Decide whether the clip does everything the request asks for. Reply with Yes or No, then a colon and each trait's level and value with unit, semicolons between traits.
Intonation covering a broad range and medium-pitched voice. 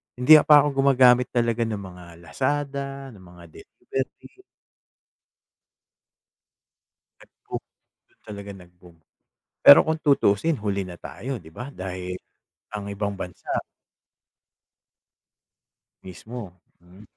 No: wide, 6.7 semitones; low, 105 Hz